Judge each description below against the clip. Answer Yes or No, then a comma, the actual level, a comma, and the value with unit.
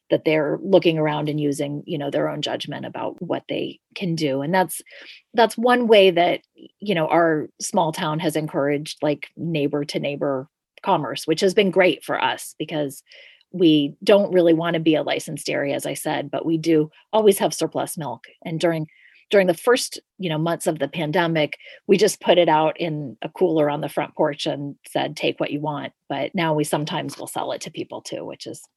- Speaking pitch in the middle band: Yes, medium, 160 Hz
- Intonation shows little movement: No, average, 3.5 semitones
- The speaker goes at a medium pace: No, fast, 210 wpm